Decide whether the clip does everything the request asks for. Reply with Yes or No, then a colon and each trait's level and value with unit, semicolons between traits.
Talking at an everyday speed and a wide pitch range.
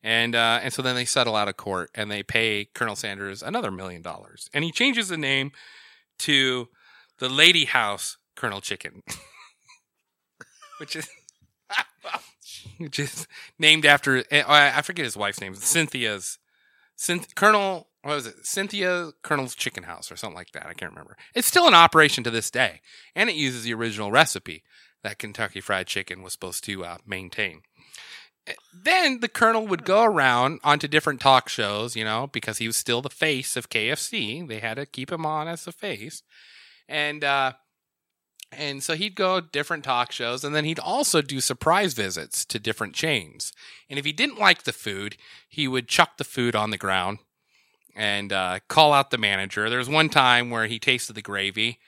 Yes: average, 185 wpm; wide, 6.1 semitones